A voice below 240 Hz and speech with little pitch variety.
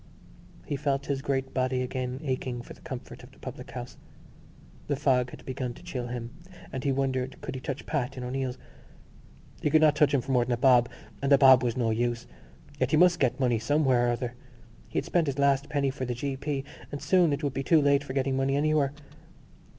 Yes: low, 135 Hz; narrow, 2.2 semitones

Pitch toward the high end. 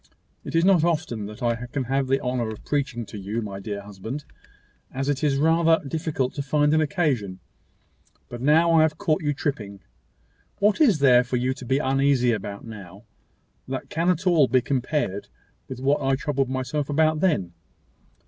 No: low, 135 Hz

